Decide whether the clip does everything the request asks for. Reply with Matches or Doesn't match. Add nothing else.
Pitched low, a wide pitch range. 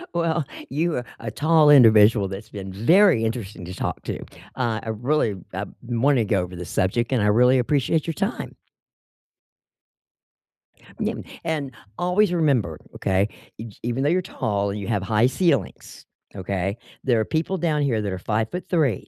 Matches